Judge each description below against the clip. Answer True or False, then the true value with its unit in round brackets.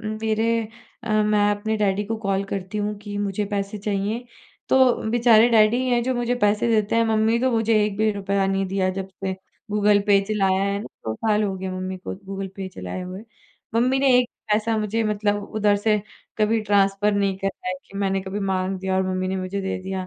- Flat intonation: True (2.0 semitones)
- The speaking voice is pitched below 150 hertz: False (205 Hz)